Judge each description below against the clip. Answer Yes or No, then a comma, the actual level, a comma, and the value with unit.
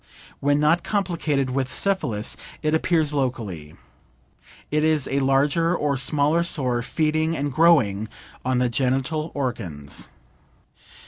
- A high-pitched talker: No, medium, 140 Hz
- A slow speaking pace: Yes, slow, 120 wpm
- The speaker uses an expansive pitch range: No, average, 3.9 semitones